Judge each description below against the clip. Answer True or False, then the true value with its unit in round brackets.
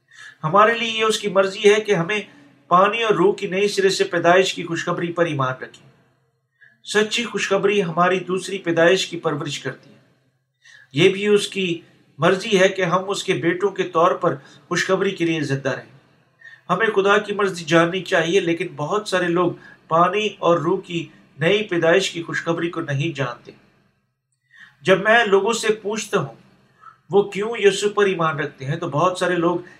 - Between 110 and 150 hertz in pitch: False (180 Hz)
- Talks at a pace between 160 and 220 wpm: True (175 wpm)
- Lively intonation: False (3.4 semitones)